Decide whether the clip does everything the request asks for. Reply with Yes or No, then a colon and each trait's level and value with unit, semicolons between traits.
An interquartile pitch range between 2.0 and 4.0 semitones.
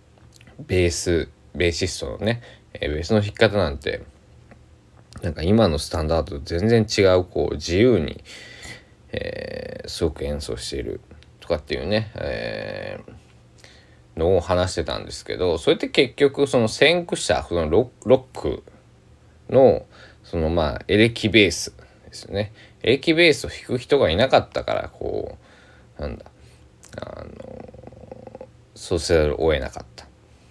No: average, 5.2 semitones